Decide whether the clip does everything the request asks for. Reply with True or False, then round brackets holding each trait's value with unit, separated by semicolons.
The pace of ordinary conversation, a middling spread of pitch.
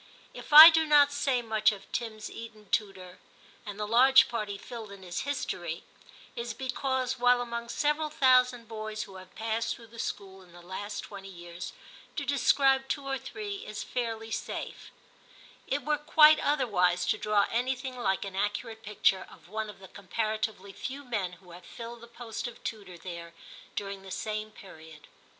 True (180 wpm; 4.8 semitones)